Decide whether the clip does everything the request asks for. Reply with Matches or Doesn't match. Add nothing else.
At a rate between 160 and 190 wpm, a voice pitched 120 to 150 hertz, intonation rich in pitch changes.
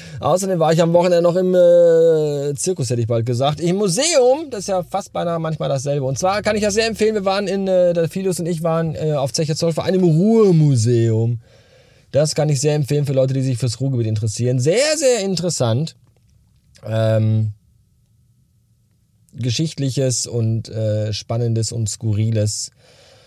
Matches